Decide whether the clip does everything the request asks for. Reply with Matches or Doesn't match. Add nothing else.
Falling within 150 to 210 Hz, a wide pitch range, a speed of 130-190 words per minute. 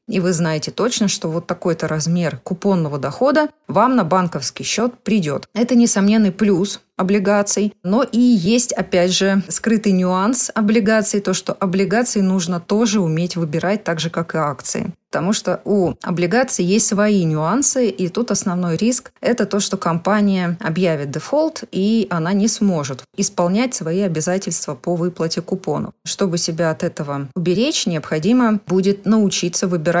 Doesn't match